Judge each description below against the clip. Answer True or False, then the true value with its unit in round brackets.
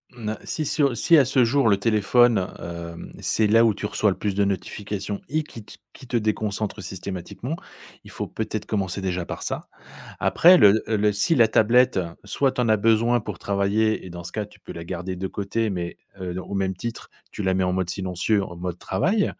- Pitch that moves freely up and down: False (3.4 semitones)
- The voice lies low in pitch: True (105 Hz)